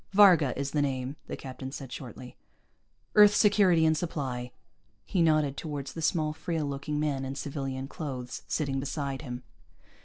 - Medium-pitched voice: Yes, medium, 145 Hz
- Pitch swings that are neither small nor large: Yes, average, 3.0 semitones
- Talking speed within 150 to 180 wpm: Yes, average, 155 wpm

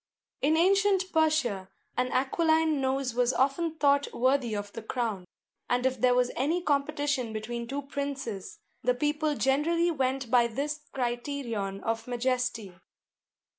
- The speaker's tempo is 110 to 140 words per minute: Yes, slow, 135 wpm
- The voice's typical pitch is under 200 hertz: No, very high, 265 Hz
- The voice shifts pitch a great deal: No, average, 3.7 semitones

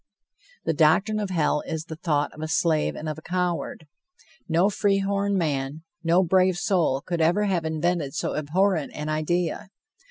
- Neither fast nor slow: Yes, average, 170 wpm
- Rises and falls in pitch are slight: No, average, 3.3 semitones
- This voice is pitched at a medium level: Yes, medium, 165 Hz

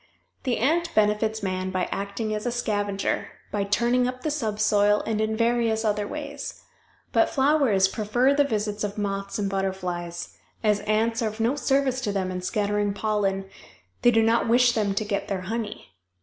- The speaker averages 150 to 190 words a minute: Yes, average, 180 wpm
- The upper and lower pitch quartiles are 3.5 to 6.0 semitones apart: No, average, 2.9 semitones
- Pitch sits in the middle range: No, high, 215 Hz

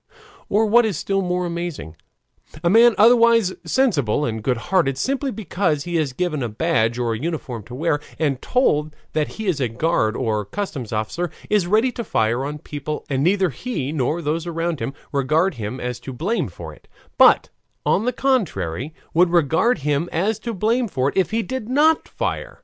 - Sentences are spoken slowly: No, average, 185 wpm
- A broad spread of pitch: Yes, wide, 7.8 semitones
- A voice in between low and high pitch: Yes, medium, 165 Hz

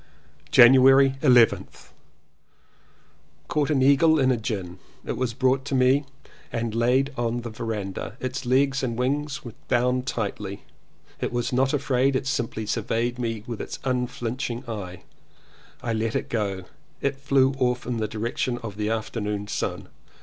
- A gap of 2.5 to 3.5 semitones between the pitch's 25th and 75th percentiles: Yes, average, 2.8 semitones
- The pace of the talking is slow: No, average, 155 wpm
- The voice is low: Yes, low, 125 Hz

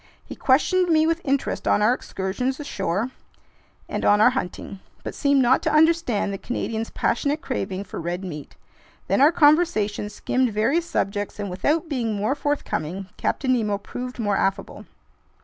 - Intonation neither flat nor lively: No, wide, 6.2 semitones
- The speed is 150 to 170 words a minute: Yes, average, 160 wpm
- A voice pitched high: Yes, high, 245 Hz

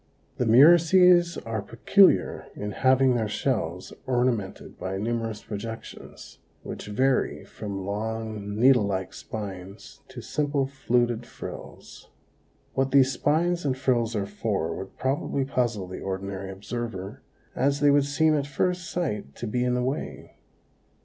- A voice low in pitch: Yes, low, 120 Hz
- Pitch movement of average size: Yes, average, 4.9 semitones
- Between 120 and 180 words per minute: Yes, slow, 135 wpm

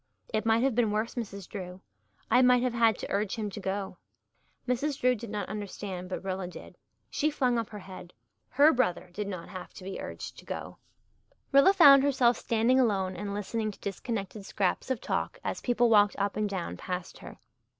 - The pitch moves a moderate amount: Yes, average, 4.0 semitones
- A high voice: Yes, high, 215 Hz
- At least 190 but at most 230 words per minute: Yes, average, 200 wpm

